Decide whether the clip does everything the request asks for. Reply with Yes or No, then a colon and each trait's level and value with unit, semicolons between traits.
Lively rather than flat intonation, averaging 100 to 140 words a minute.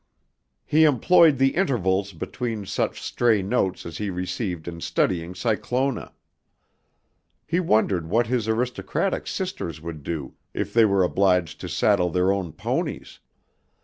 Yes: wide, 5.7 semitones; slow, 135 wpm